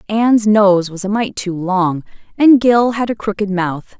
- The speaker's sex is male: No, female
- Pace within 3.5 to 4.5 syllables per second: Yes, 4.3 syllables/s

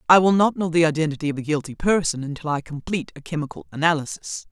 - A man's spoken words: No, female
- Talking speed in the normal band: No, fast, 215 wpm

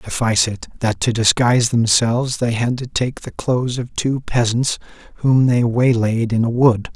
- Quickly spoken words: No, average, 180 wpm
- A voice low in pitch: Yes, low, 120 Hz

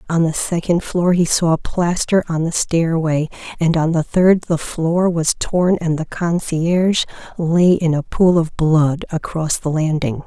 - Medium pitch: Yes, medium, 165 Hz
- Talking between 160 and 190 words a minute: Yes, average, 175 wpm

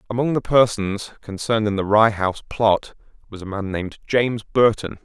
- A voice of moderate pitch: No, low, 110 Hz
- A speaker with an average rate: Yes, average, 180 wpm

